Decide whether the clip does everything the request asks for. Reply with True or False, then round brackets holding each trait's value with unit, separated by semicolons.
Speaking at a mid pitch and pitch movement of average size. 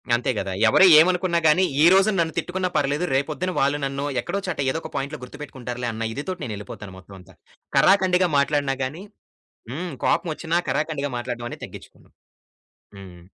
False (145 Hz; 6.1 semitones)